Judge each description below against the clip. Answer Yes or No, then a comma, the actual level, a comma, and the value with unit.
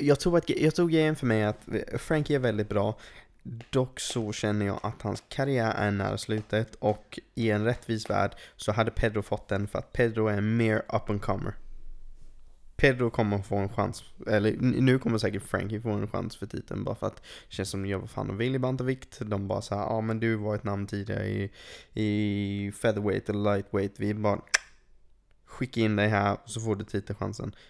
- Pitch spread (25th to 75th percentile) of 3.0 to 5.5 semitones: No, narrow, 2.5 semitones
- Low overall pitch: Yes, low, 110 Hz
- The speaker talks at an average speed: No, fast, 210 wpm